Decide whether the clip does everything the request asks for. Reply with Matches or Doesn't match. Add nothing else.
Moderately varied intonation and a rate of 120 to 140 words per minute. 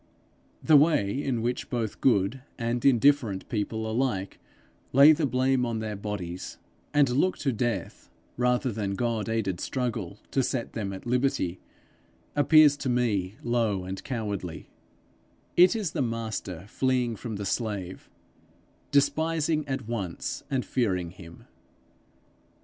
Matches